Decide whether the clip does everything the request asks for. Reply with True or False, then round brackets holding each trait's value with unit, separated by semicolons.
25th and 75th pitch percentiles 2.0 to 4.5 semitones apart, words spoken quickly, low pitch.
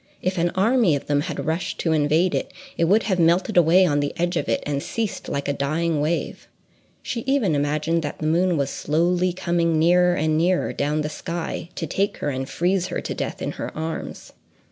False (3.0 semitones; 210 wpm; 165 Hz)